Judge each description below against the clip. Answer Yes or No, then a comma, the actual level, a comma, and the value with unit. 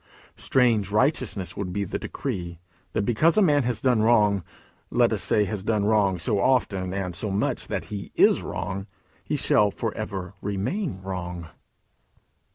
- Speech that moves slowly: No, average, 165 wpm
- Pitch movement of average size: Yes, average, 3.7 semitones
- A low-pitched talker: Yes, low, 100 Hz